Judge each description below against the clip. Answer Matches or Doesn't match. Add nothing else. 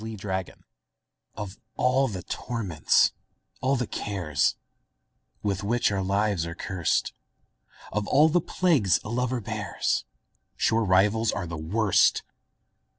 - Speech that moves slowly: Matches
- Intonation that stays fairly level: Doesn't match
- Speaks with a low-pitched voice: Matches